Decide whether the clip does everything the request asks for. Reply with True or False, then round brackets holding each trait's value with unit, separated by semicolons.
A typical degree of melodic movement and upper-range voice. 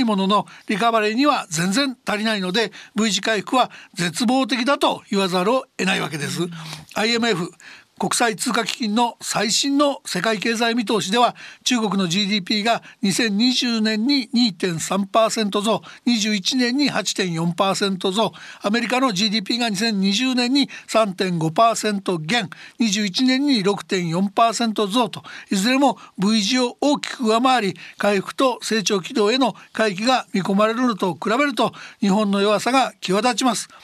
True (3.5 semitones; 220 Hz)